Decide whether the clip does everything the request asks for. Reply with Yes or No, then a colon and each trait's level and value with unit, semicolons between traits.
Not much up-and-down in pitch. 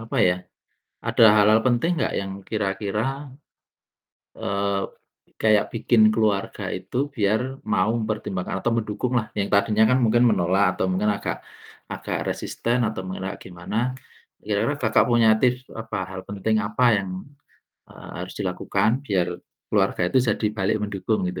Yes: narrow, 2.3 semitones